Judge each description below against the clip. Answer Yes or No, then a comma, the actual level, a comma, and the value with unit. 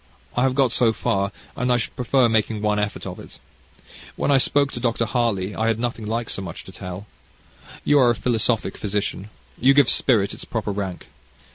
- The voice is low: Yes, low, 115 Hz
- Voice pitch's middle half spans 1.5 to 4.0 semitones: Yes, average, 3.1 semitones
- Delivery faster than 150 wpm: Yes, fast, 205 wpm